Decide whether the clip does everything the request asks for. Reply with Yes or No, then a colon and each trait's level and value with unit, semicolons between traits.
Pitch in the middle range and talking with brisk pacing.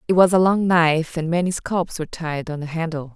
Yes: medium, 165 Hz; fast, 245 wpm